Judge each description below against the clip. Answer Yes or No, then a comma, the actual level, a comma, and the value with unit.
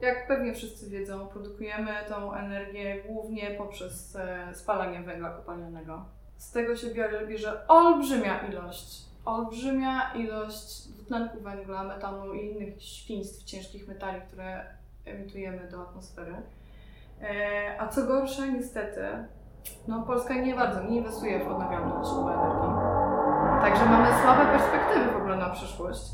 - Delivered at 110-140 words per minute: Yes, average, 130 wpm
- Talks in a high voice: Yes, high, 205 Hz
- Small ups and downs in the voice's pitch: No, average, 3.0 semitones